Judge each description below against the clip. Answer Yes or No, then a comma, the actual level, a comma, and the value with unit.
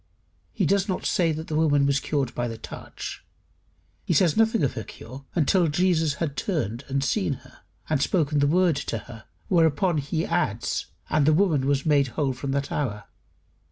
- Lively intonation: No, average, 3.6 semitones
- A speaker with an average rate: Yes, average, 190 wpm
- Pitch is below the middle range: No, medium, 145 Hz